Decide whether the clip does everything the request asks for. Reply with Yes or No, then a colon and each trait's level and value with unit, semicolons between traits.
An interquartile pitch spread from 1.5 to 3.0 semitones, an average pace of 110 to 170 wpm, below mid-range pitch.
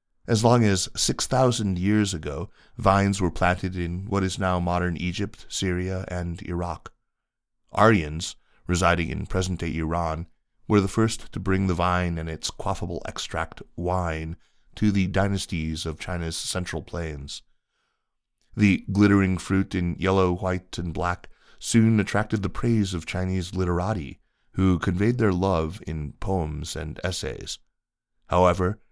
Yes: narrow, 2.5 semitones; average, 140 wpm; very low, 90 Hz